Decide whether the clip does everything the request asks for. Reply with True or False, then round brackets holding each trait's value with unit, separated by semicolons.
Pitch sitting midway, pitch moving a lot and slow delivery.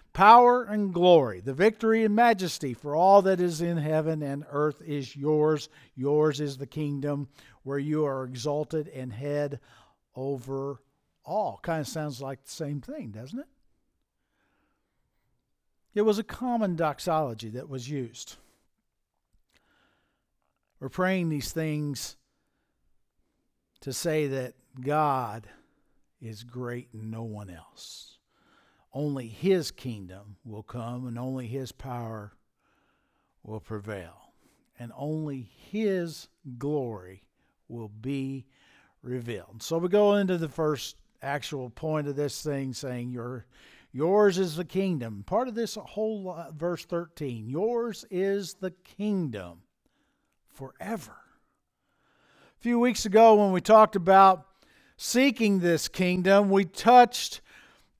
True (150 Hz; 6.4 semitones; 125 wpm)